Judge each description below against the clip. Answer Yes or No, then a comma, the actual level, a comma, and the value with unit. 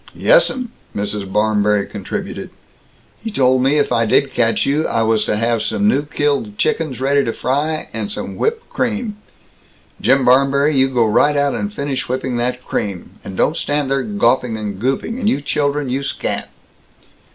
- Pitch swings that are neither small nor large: Yes, average, 4.4 semitones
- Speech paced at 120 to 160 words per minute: No, average, 175 wpm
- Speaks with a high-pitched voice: No, low, 135 Hz